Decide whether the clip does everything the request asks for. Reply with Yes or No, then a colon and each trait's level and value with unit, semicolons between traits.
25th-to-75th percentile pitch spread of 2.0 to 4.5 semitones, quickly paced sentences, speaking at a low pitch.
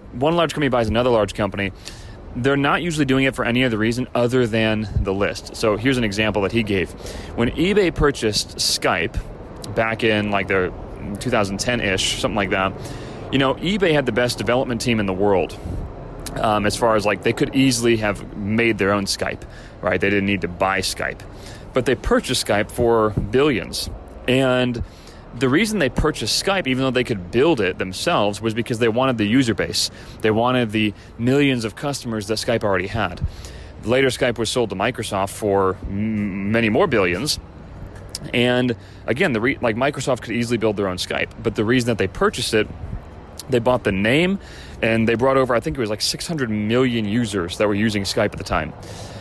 No: average, 3.8 semitones; average, 195 wpm; low, 110 Hz